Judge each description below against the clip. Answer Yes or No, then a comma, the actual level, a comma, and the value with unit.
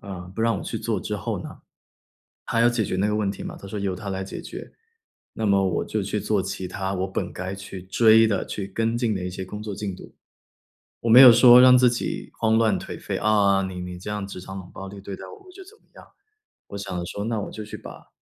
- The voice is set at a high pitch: No, low, 100 Hz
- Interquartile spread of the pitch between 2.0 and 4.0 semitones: Yes, average, 2.9 semitones